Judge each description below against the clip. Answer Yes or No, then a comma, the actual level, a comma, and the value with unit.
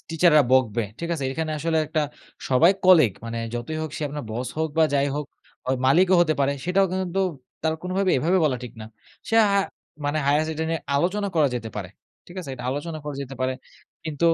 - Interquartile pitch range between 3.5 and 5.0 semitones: Yes, average, 4.0 semitones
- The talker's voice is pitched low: No, medium, 155 Hz